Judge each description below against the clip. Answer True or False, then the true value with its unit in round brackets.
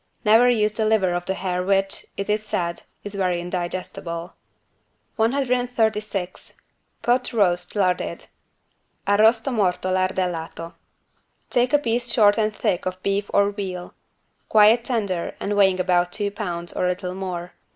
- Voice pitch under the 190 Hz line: False (200 Hz)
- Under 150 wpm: True (140 wpm)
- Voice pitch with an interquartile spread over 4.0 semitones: False (3.2 semitones)